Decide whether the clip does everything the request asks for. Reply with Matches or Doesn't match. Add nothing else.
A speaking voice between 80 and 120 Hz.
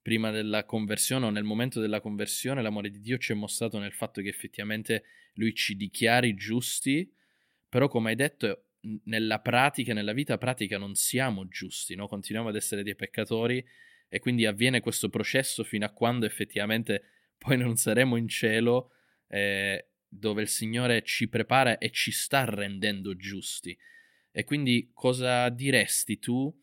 Matches